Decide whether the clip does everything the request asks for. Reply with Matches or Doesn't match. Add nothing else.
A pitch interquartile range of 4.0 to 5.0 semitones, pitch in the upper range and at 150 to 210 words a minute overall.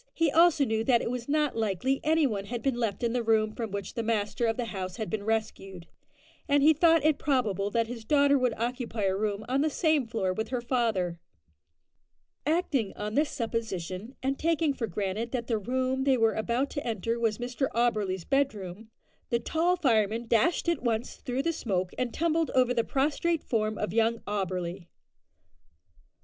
Matches